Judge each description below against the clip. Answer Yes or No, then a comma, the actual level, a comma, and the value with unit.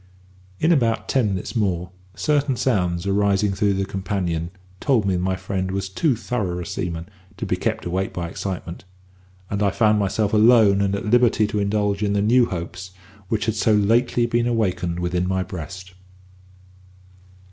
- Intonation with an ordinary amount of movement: Yes, average, 3.2 semitones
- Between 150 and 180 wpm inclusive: Yes, average, 170 wpm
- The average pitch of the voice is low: Yes, low, 100 Hz